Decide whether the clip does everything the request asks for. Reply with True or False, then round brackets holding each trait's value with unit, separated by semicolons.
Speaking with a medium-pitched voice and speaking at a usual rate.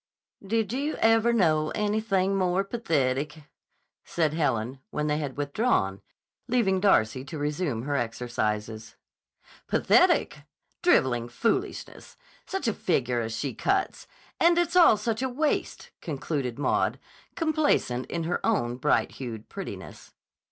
False (155 Hz; 125 wpm)